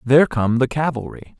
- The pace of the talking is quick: No, average, 175 wpm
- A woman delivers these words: No, male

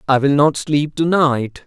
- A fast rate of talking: Yes, fast, 215 wpm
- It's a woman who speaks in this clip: No, male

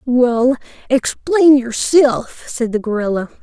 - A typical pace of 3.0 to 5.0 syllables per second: Yes, 3.5 syllables/s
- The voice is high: Yes, very high, 250 Hz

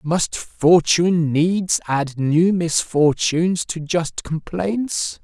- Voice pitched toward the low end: No, medium, 160 Hz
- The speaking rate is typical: No, slow, 105 wpm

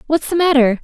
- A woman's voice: Yes, female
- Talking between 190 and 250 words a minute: Yes, fast, 215 wpm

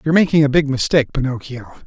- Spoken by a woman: No, male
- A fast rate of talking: Yes, fast, 225 wpm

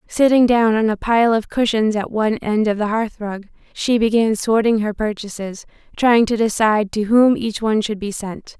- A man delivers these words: No, female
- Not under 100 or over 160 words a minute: No, fast, 205 wpm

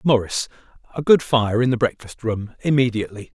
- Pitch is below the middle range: Yes, low, 120 Hz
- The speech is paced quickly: No, average, 160 wpm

